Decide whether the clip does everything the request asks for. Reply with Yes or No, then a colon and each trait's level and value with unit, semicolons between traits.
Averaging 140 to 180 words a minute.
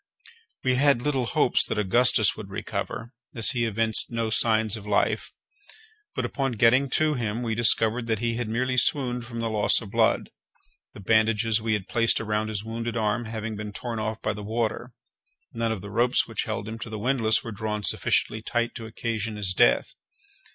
No: average, 195 wpm